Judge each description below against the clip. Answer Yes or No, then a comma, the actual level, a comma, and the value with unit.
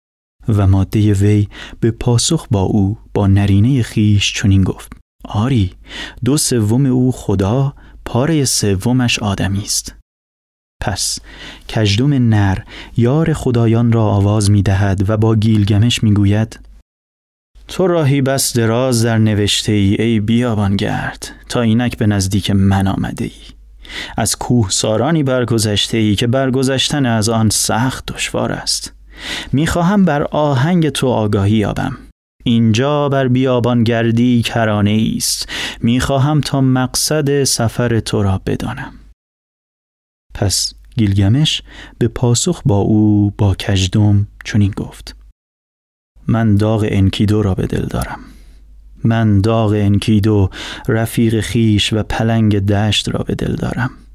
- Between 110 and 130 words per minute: Yes, average, 125 wpm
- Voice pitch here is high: No, low, 110 Hz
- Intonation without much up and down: No, average, 3.6 semitones